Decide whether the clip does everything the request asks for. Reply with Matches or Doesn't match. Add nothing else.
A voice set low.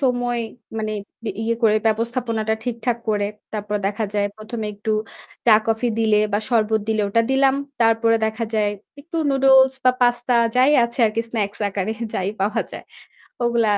Doesn't match